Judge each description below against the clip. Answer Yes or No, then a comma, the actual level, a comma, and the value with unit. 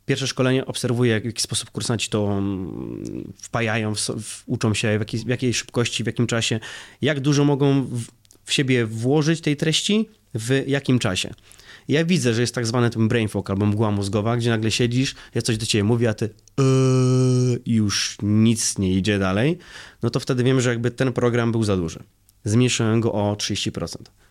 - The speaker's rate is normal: No, fast, 190 wpm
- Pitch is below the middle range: Yes, low, 120 Hz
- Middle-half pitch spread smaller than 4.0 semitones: Yes, average, 3.2 semitones